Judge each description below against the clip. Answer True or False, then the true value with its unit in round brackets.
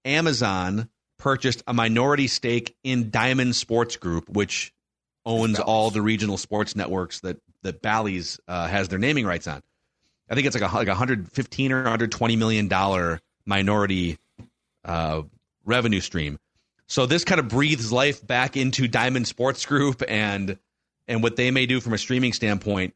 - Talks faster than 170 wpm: False (160 wpm)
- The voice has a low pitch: True (115 Hz)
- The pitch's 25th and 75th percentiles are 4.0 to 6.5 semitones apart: True (4.5 semitones)